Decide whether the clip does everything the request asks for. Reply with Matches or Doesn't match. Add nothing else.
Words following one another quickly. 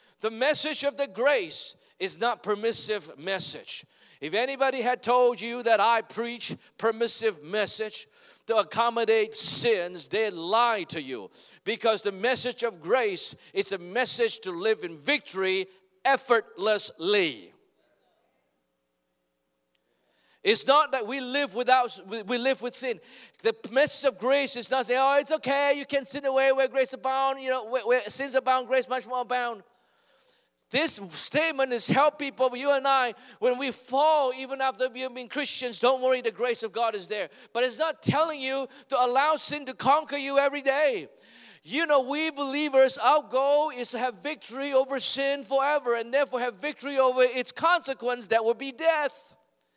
Doesn't match